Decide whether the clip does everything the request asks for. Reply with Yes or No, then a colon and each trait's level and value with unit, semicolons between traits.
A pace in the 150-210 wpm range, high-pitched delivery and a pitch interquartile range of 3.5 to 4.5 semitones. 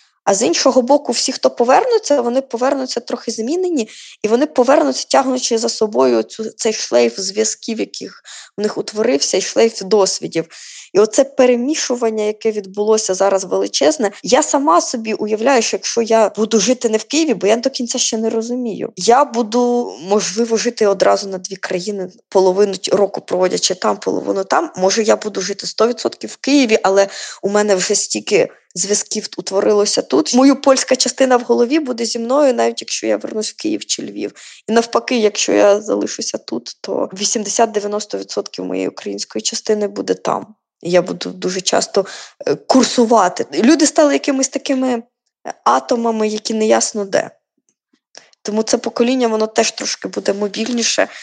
Yes: fast, 155 wpm; high, 225 Hz; average, 4.0 semitones